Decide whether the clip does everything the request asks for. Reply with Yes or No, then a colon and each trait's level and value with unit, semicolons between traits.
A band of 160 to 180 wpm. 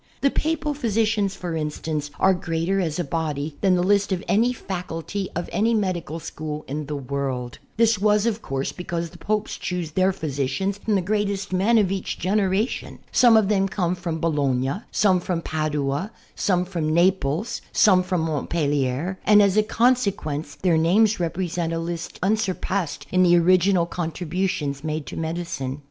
Yes: average, 165 wpm